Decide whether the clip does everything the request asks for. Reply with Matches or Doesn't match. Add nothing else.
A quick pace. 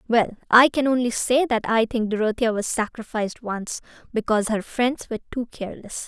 Doesn't match